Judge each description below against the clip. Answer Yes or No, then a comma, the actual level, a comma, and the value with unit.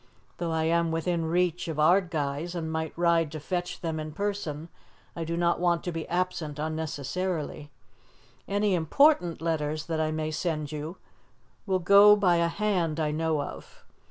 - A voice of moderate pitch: Yes, medium, 165 Hz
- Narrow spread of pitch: Yes, narrow, 2.3 semitones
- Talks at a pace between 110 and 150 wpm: No, average, 165 wpm